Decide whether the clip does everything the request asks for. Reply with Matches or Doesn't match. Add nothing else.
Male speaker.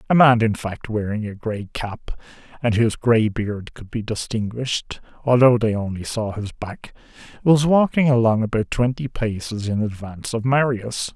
Matches